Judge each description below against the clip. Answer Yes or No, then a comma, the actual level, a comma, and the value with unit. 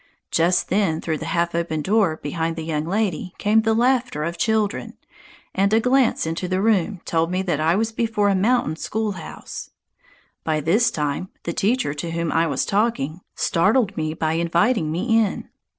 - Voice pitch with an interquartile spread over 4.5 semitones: Yes, average, 5.2 semitones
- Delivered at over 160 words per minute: Yes, average, 180 wpm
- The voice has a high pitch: No, medium, 180 Hz